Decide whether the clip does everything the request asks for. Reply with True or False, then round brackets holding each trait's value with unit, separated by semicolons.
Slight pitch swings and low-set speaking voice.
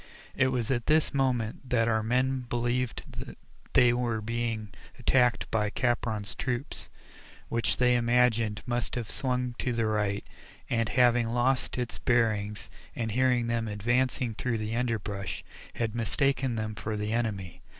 True (2.1 semitones; 120 Hz)